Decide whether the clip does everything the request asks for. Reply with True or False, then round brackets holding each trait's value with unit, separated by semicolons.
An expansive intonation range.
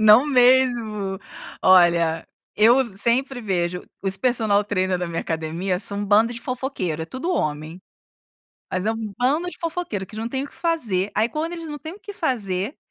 True (5.9 semitones)